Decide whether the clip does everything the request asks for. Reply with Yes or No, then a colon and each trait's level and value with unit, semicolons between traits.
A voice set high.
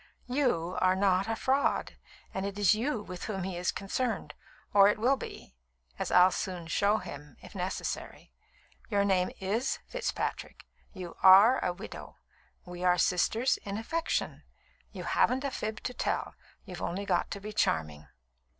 Yes: high, 200 Hz